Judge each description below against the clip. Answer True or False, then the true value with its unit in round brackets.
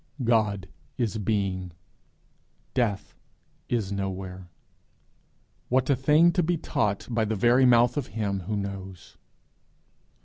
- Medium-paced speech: False (115 wpm)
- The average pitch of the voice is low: True (110 Hz)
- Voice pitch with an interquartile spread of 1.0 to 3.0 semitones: False (4.0 semitones)